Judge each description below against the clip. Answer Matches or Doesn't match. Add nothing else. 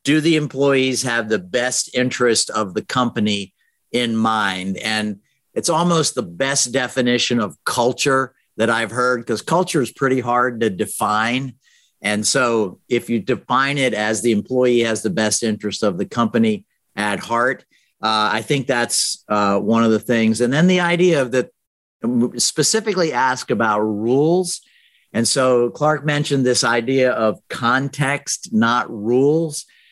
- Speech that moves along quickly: Doesn't match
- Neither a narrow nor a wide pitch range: Matches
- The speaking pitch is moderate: Doesn't match